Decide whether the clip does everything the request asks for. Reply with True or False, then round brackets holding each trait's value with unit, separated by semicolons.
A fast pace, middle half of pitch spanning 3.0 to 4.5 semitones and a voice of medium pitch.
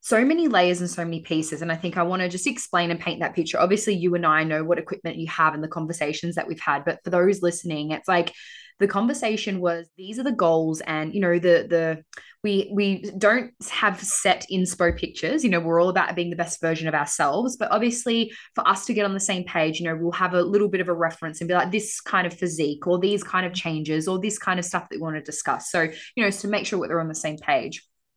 True (265 wpm; 3.4 semitones; 180 Hz)